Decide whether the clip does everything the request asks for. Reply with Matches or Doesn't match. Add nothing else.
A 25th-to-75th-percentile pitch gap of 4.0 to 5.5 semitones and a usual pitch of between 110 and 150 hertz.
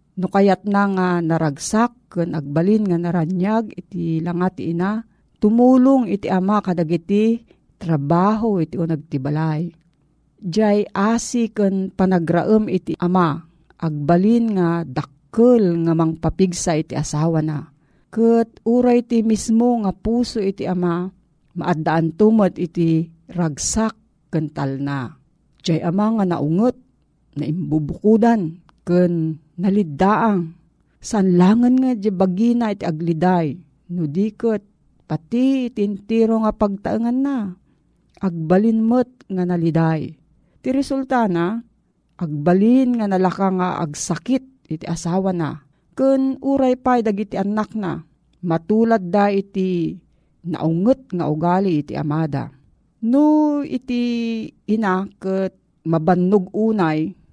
Doesn't match